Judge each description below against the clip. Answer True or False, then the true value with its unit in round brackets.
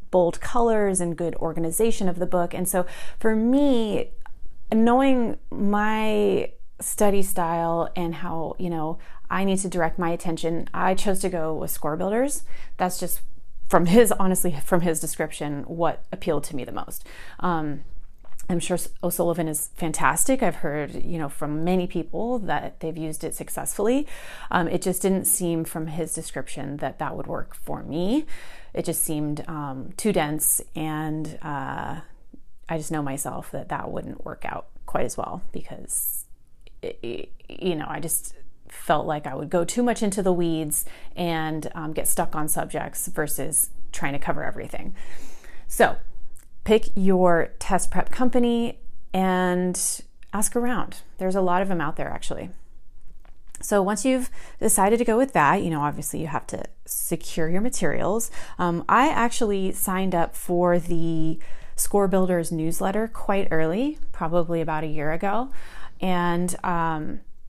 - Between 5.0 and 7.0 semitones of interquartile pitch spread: False (3.9 semitones)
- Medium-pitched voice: True (175 Hz)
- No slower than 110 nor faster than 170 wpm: True (160 wpm)